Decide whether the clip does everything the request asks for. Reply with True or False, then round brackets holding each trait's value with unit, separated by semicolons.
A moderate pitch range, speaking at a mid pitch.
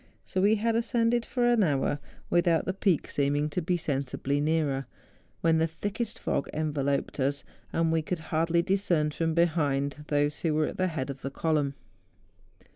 True (3.9 semitones; 160 Hz)